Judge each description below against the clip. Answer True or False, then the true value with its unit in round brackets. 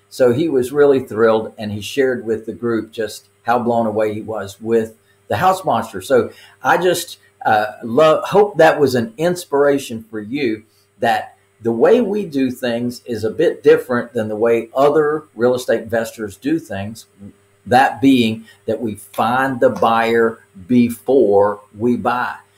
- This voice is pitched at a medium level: False (115 Hz)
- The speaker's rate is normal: True (165 wpm)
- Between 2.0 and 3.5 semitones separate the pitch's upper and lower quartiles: False (4.6 semitones)